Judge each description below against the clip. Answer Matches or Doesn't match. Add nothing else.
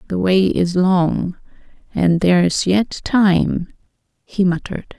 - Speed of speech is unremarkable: Doesn't match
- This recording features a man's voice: Doesn't match